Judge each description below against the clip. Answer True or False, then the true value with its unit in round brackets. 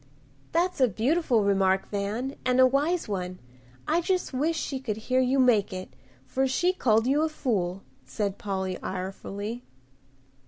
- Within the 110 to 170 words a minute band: True (155 wpm)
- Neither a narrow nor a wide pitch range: False (5.7 semitones)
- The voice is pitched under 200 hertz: False (240 Hz)